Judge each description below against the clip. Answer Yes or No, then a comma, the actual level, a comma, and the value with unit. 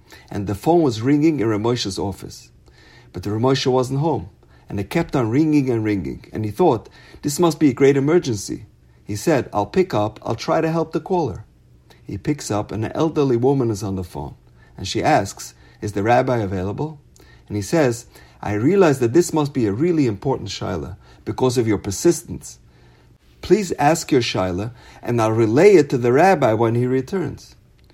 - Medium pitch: No, low, 120 Hz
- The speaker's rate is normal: Yes, average, 190 wpm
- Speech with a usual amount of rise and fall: No, wide, 6.2 semitones